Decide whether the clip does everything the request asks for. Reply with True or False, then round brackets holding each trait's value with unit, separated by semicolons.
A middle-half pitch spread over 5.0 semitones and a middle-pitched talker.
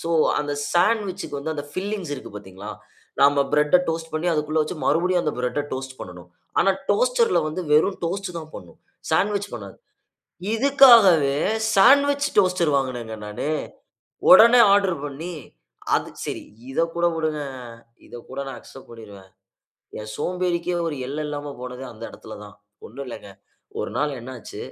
True (5.6 semitones; 155 Hz)